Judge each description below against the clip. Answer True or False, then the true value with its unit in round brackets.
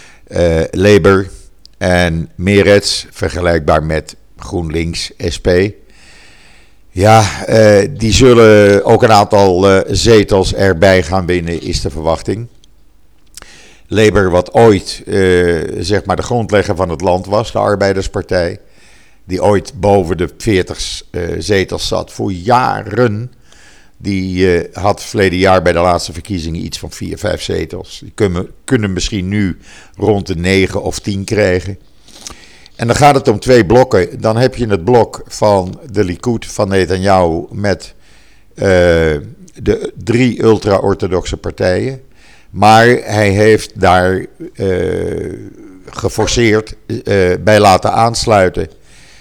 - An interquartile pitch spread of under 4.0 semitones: True (3.2 semitones)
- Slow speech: True (125 wpm)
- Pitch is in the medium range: False (100 Hz)